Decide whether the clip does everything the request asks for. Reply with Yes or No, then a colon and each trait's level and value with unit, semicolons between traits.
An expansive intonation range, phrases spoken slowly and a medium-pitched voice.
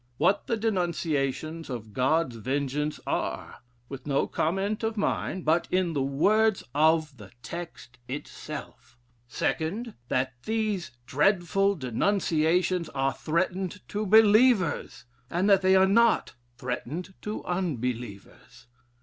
Yes: wide, 6.2 semitones; slow, 115 wpm; medium, 165 Hz